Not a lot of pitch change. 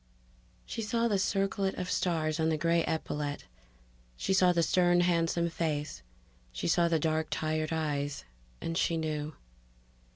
Yes: narrow, 2.2 semitones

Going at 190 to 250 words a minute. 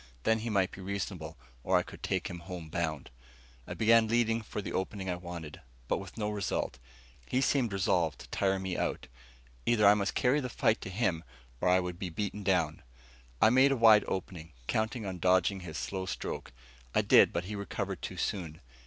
Yes: average, 200 wpm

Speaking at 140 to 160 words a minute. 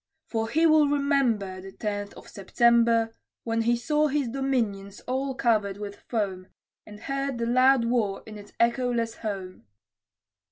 Yes: average, 150 wpm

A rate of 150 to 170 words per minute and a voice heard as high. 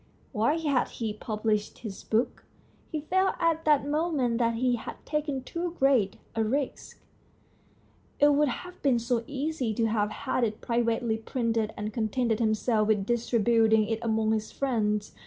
Yes: average, 155 wpm; high, 235 Hz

